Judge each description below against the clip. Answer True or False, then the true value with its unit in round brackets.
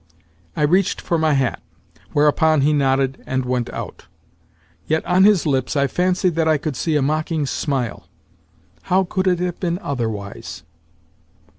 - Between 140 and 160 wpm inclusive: True (155 wpm)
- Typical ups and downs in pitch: True (4.5 semitones)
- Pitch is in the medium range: True (150 Hz)